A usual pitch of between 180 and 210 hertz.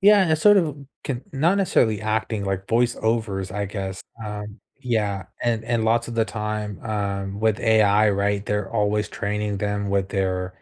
No: low, 105 Hz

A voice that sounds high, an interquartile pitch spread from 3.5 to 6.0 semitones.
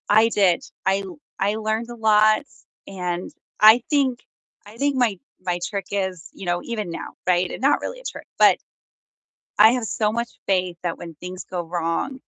Yes: high, 205 Hz; average, 4.1 semitones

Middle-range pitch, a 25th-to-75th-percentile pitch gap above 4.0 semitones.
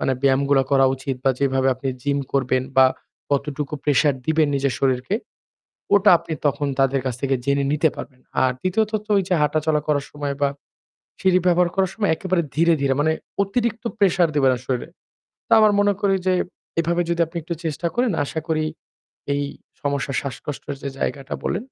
Yes: medium, 145 Hz; average, 4.4 semitones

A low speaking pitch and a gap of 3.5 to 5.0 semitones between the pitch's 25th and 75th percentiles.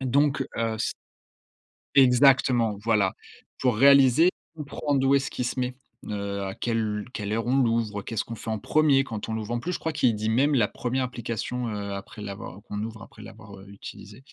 Yes: low, 115 Hz; average, 4.0 semitones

